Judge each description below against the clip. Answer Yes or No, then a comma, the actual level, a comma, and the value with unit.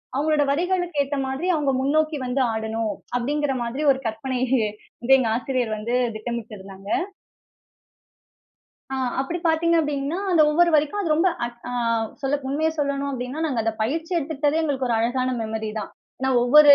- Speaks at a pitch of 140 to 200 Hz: No, very high, 275 Hz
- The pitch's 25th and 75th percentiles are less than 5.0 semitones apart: Yes, average, 4.2 semitones